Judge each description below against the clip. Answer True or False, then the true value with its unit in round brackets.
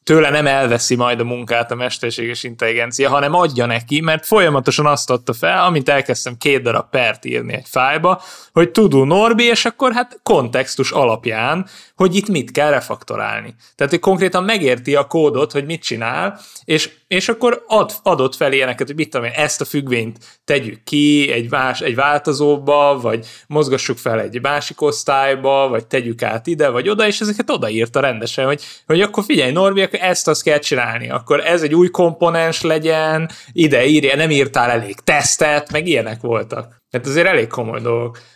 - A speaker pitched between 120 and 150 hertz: True (140 Hz)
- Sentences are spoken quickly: True (175 wpm)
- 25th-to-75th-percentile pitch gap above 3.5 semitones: True (5.1 semitones)